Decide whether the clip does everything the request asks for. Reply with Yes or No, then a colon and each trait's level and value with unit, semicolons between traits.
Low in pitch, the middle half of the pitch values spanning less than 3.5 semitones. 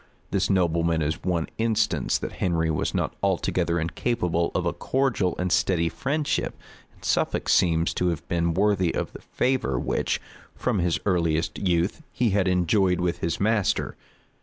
Yes: very low, 90 Hz; average, 3.1 semitones